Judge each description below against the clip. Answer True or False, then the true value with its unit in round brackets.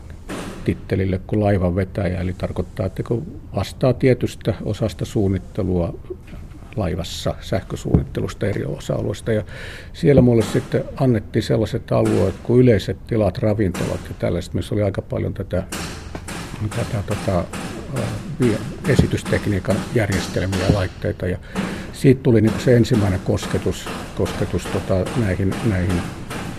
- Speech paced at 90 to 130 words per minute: True (120 wpm)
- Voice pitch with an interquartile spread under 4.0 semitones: True (3.3 semitones)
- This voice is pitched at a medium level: False (100 Hz)